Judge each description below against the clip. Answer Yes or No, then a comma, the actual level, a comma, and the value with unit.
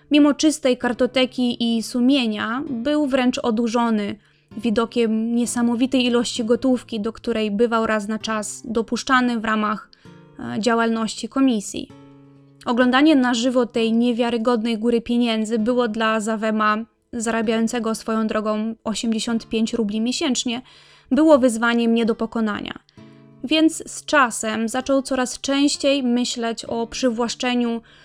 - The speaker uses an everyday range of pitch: No, narrow, 2.2 semitones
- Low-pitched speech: No, high, 235 Hz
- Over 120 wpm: No, average, 115 wpm